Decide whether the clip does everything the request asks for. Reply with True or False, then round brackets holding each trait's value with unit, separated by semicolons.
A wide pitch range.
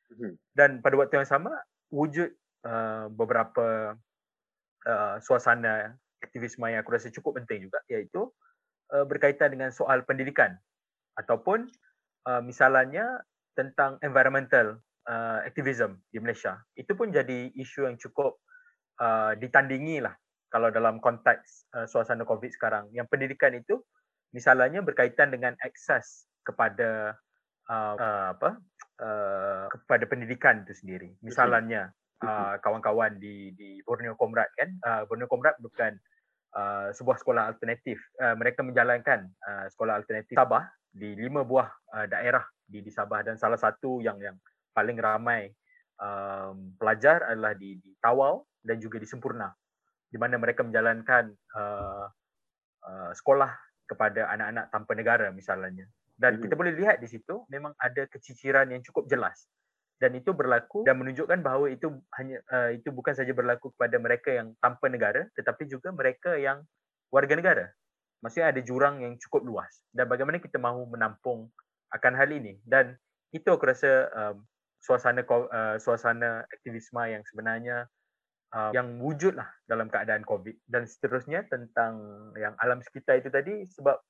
False (3.8 semitones)